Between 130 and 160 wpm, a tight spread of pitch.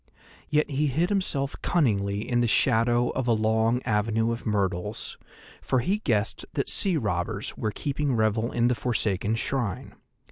No: average, 155 wpm; average, 3.9 semitones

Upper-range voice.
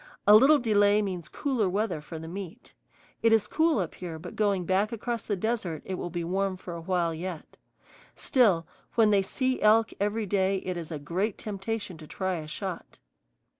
Yes: high, 195 Hz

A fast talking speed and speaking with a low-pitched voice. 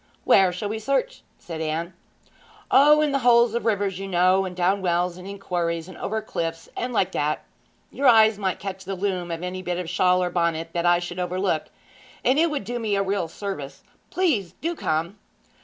No: fast, 210 wpm; high, 190 Hz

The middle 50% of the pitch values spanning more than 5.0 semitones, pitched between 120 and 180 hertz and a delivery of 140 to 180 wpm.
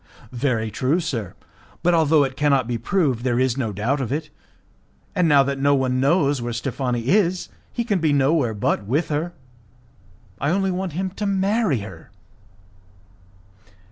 Yes: wide, 5.6 semitones; medium, 140 Hz; average, 165 wpm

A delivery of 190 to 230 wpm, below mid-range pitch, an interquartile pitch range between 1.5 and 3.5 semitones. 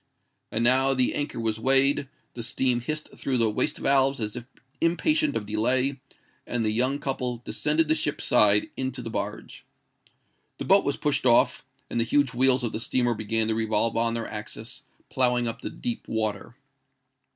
No: average, 175 wpm; low, 125 Hz; average, 3.2 semitones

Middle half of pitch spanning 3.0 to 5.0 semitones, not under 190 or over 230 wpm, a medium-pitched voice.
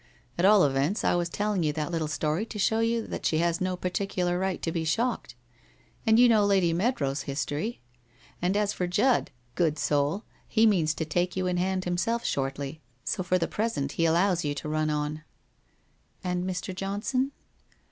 Yes: average, 4.6 semitones; average, 195 wpm; medium, 180 Hz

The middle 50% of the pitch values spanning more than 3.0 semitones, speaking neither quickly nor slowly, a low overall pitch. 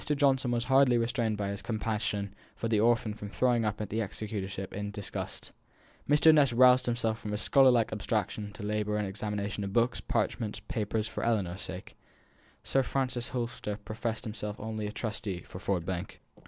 No: average, 2.7 semitones; average, 180 wpm; low, 110 Hz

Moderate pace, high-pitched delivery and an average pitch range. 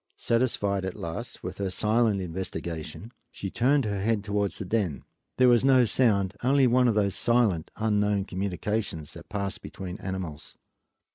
No: average, 155 wpm; low, 100 Hz; average, 3.7 semitones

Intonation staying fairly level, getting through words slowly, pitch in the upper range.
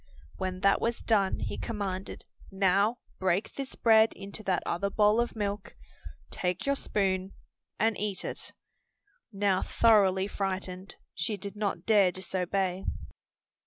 Yes: narrow, 2.1 semitones; slow, 130 wpm; high, 195 Hz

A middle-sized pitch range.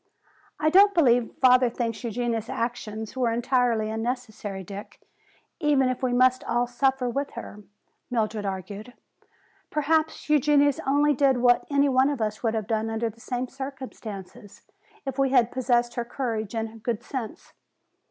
Yes: average, 3.2 semitones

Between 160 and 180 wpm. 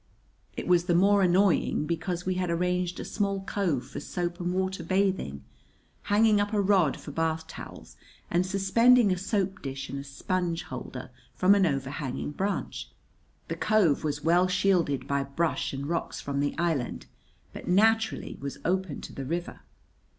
Yes: average, 165 wpm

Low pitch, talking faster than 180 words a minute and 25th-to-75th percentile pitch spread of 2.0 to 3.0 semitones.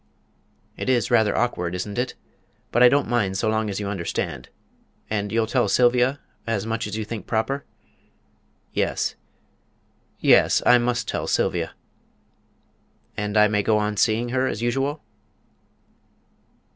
No: low, 110 Hz; average, 140 wpm; average, 2.7 semitones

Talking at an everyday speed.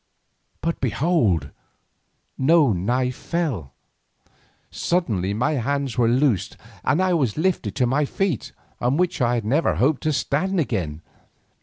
No: slow, 130 wpm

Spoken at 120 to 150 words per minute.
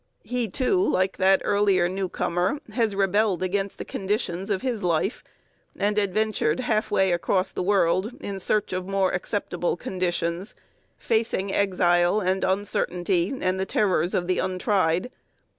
Yes: average, 140 wpm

